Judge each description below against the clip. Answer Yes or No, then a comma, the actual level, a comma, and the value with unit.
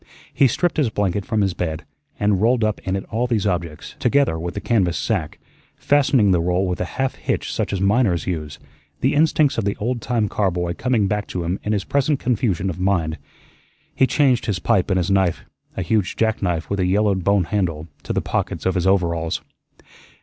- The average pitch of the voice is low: Yes, low, 100 Hz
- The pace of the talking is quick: Yes, fast, 210 wpm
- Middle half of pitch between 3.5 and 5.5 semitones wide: Yes, average, 4.3 semitones